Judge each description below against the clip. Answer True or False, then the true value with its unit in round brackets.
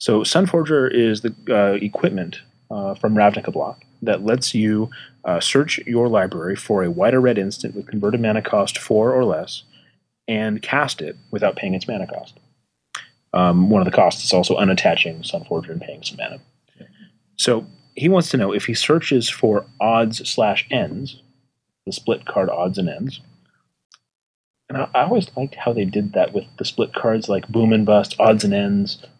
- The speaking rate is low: False (185 wpm)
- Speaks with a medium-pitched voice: False (115 Hz)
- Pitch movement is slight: False (3.9 semitones)